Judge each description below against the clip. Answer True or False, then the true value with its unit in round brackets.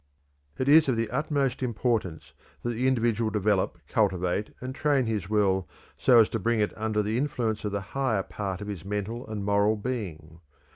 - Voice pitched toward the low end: True (110 Hz)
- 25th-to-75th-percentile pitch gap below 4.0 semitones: True (3.3 semitones)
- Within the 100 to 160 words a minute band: False (185 wpm)